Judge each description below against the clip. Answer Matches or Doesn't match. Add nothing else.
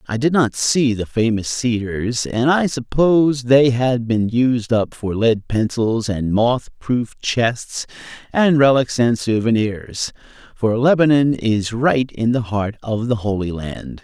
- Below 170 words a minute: Matches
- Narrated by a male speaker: Matches